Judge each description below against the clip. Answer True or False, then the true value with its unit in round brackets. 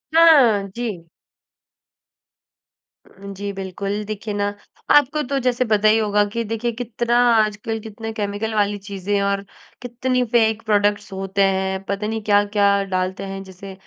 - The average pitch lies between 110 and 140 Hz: False (205 Hz)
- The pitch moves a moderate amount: False (2.2 semitones)